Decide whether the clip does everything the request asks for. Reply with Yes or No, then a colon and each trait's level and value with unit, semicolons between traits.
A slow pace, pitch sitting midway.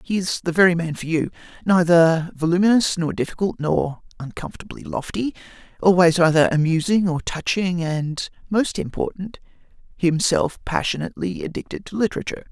Yes: slow, 120 wpm; medium, 170 Hz